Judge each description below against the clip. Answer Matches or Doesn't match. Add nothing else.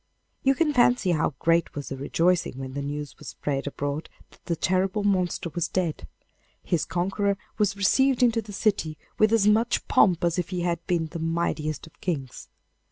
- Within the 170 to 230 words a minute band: Matches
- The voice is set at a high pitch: Doesn't match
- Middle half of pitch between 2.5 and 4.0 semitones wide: Doesn't match